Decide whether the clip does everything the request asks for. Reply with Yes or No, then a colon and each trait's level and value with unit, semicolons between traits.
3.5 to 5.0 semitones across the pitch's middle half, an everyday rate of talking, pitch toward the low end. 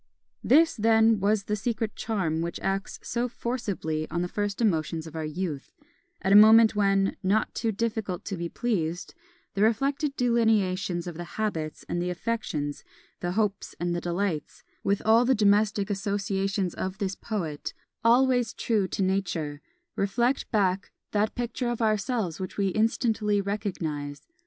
No: average, 3.9 semitones; average, 155 wpm; high, 200 Hz